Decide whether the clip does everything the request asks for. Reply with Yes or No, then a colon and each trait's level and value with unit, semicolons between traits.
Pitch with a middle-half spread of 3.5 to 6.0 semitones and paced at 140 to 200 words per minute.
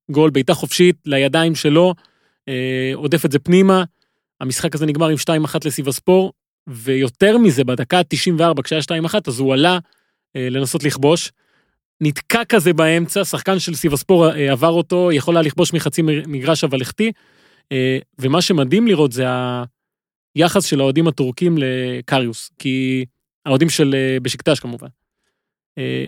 Yes: average, 4.3 semitones; average, 145 wpm